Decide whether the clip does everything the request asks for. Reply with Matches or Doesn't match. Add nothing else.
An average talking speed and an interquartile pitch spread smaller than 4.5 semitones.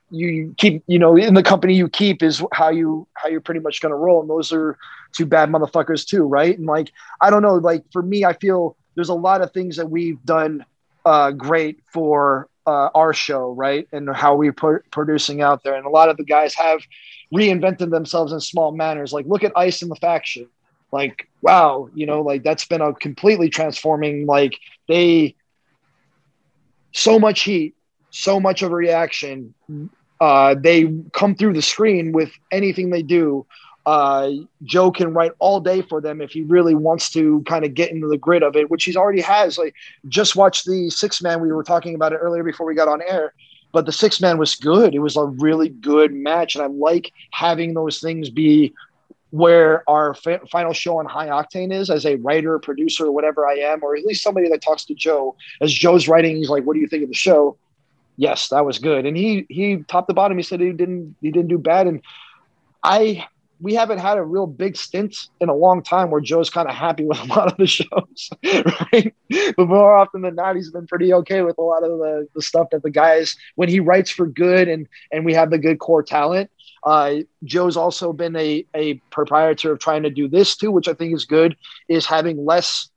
Doesn't match